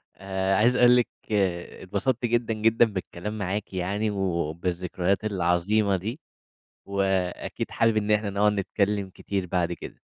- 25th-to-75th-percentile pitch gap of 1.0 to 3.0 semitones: Yes, average, 2.7 semitones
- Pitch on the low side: Yes, low, 100 Hz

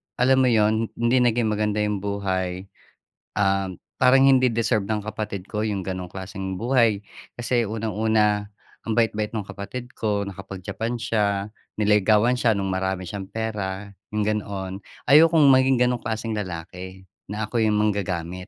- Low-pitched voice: Yes, low, 105 Hz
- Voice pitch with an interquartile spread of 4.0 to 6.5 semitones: No, average, 2.7 semitones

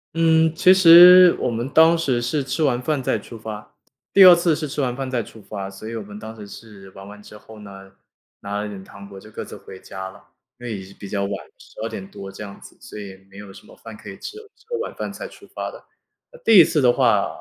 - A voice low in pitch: Yes, low, 115 Hz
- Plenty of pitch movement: Yes, wide, 7.8 semitones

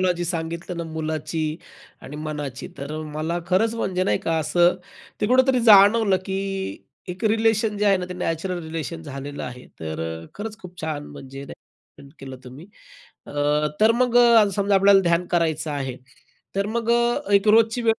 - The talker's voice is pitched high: No, medium, 175 Hz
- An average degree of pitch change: Yes, average, 5.0 semitones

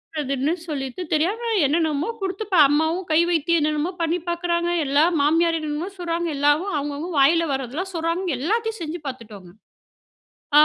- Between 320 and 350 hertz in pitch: Yes, very high, 325 Hz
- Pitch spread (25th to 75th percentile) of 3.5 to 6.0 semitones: No, average, 3.1 semitones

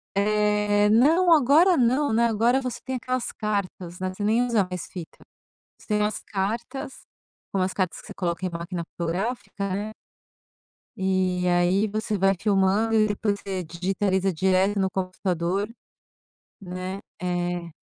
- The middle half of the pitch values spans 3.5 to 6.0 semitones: No, average, 3.1 semitones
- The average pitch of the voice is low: No, high, 200 Hz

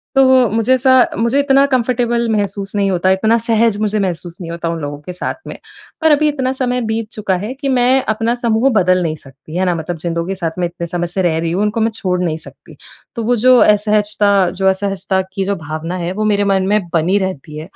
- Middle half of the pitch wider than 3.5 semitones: Yes, average, 4.7 semitones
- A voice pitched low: No, high, 200 Hz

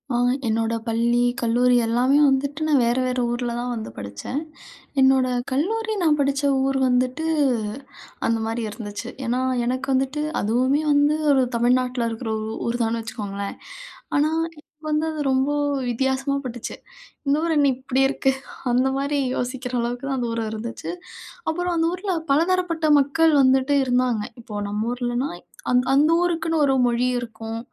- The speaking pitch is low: No, very high, 255 Hz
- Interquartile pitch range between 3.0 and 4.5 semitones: Yes, average, 3.3 semitones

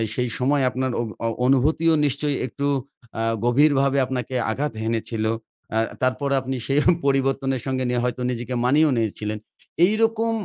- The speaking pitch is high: No, low, 130 Hz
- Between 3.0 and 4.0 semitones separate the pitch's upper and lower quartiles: No, narrow, 2.4 semitones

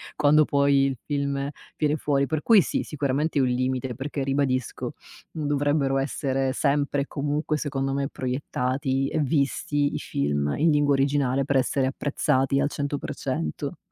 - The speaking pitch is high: No, medium, 140 Hz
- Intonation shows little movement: Yes, narrow, 1.4 semitones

